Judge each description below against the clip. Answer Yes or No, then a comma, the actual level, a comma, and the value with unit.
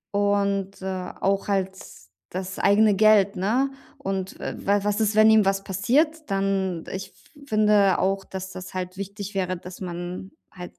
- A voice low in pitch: No, high, 195 Hz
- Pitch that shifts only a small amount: Yes, narrow, 1.6 semitones